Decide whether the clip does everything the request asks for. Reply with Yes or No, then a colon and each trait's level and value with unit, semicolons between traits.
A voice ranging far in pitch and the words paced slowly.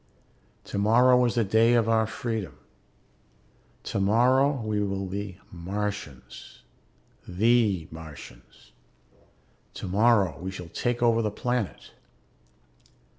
No: average, 3.8 semitones; slow, 95 wpm